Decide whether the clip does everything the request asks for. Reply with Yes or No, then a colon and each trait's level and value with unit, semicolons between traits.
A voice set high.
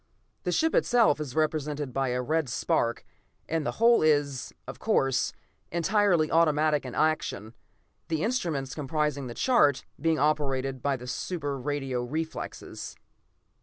No: medium, 150 Hz